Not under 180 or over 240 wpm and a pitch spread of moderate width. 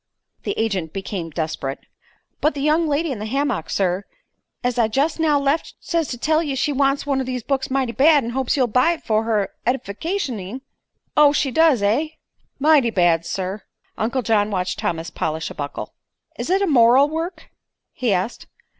No: average, 185 wpm; wide, 6.2 semitones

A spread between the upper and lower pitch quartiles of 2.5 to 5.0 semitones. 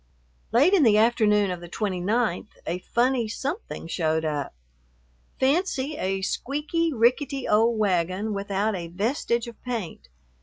No: wide, 5.5 semitones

